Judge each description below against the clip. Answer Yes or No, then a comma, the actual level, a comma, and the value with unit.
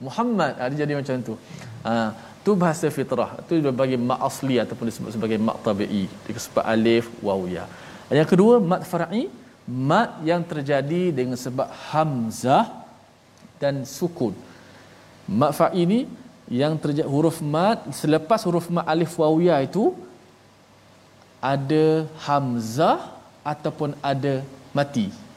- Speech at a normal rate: No, fast, 130 wpm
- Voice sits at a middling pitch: Yes, medium, 145 Hz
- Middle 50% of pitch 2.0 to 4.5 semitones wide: No, wide, 5.5 semitones